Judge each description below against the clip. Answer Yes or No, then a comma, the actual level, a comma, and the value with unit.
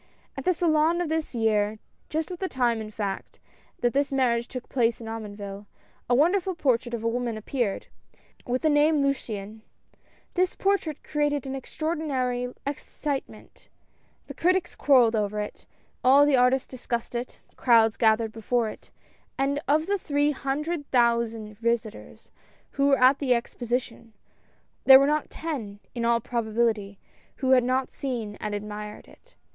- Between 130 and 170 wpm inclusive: Yes, average, 160 wpm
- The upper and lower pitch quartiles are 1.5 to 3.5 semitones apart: No, average, 4.3 semitones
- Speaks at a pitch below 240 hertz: No, very high, 250 Hz